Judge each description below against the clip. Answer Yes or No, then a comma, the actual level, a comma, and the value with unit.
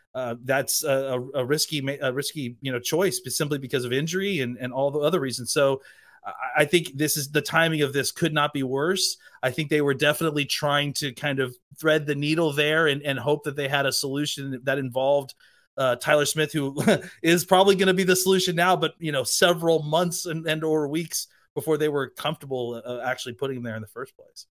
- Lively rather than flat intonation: No, average, 3.0 semitones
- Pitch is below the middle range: No, medium, 150 Hz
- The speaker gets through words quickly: Yes, fast, 225 wpm